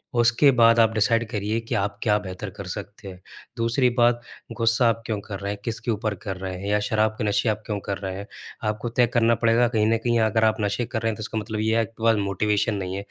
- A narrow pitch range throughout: Yes, narrow, 2.1 semitones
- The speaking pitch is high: No, low, 110 Hz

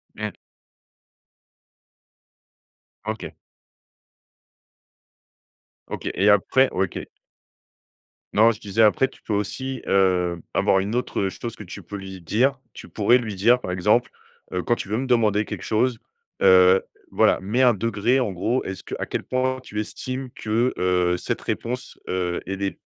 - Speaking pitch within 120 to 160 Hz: No, low, 105 Hz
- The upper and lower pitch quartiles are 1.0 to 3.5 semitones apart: No, average, 4.3 semitones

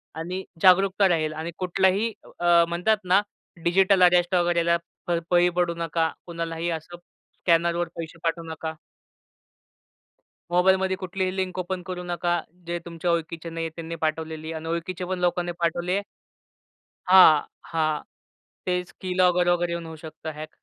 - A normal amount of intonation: No, narrow, 1.6 semitones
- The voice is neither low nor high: Yes, medium, 175 Hz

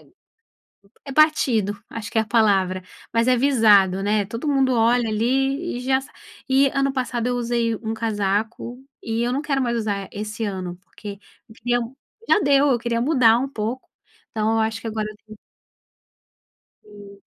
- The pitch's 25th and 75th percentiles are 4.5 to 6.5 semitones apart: No, average, 3.4 semitones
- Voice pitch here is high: Yes, high, 230 Hz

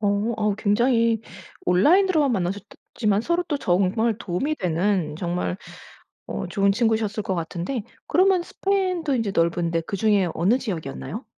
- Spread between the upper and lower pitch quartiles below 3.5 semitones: No, wide, 5.5 semitones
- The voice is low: No, high, 210 Hz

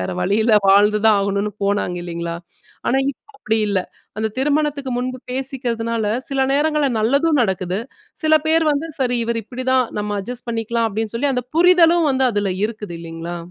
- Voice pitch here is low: No, high, 230 Hz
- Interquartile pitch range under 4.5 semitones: No, average, 4.8 semitones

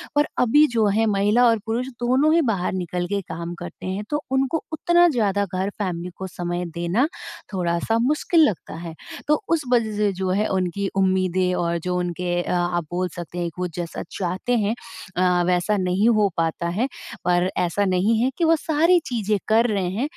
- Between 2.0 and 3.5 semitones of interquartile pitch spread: No, average, 4.8 semitones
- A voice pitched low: No, high, 195 Hz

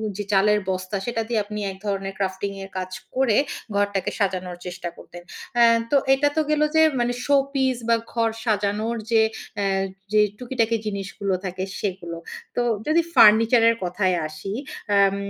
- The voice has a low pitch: No, high, 205 Hz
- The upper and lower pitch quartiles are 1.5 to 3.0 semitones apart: No, average, 3.6 semitones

